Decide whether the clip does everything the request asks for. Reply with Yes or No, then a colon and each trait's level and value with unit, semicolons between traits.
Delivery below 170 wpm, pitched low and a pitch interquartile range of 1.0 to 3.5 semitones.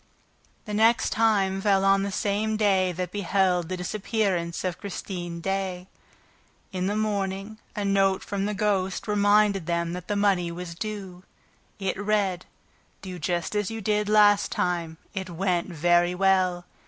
No: average, 155 wpm; high, 195 Hz; narrow, 2.4 semitones